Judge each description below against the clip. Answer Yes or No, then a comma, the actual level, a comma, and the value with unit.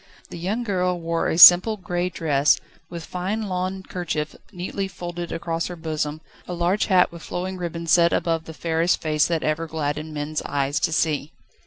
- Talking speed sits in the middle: Yes, average, 180 wpm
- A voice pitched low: No, medium, 170 Hz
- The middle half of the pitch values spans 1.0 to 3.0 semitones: Yes, narrow, 2.4 semitones